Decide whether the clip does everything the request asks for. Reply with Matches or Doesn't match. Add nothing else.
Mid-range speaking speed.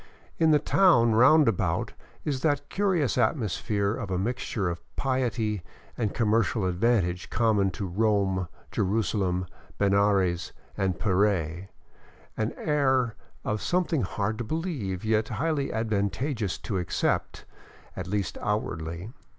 Doesn't match